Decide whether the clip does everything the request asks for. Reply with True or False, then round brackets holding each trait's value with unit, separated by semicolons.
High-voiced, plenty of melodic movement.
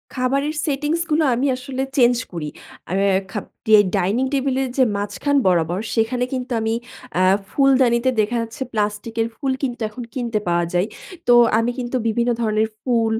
False (235 Hz; 3.5 semitones)